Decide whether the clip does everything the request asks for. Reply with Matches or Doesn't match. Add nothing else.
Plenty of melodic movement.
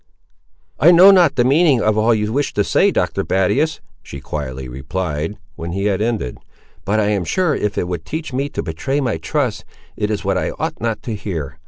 Matches